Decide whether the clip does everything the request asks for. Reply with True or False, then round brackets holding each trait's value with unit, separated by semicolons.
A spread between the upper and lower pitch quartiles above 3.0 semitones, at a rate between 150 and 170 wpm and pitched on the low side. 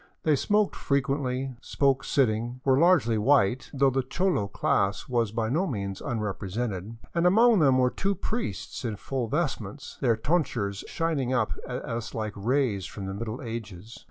True (4.5 semitones; 160 wpm; 125 Hz)